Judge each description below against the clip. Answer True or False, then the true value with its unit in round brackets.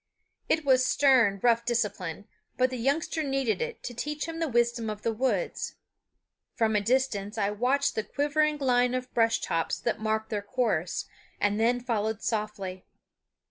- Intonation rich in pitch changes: False (3.8 semitones)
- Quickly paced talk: False (165 wpm)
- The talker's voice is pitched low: False (235 Hz)